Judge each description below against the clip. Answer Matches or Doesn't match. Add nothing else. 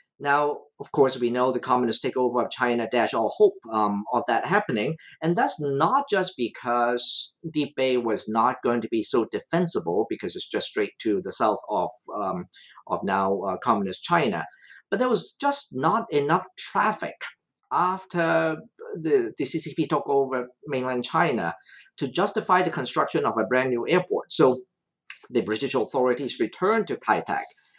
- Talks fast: Doesn't match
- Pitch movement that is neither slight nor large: Doesn't match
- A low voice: Doesn't match